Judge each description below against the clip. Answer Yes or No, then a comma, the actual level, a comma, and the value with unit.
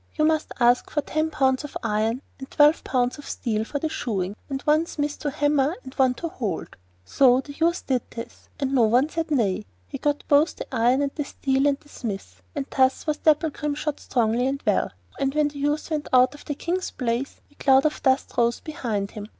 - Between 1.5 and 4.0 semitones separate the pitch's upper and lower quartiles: Yes, average, 3.4 semitones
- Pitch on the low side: No, very high, 275 Hz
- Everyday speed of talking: No, fast, 225 wpm